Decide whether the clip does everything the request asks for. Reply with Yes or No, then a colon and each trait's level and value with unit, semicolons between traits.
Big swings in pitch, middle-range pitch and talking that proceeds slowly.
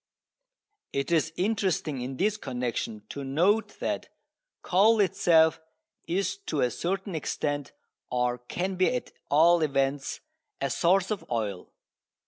Yes: wide, 6.1 semitones; medium, 160 Hz; slow, 125 wpm